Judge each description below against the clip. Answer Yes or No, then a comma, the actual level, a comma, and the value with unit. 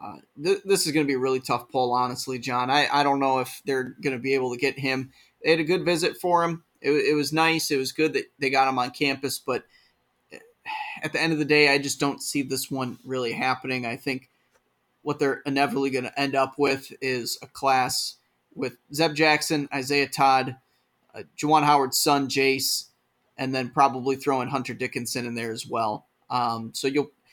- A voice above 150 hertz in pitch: No, low, 135 Hz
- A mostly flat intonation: Yes, narrow, 2.2 semitones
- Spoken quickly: Yes, fast, 215 wpm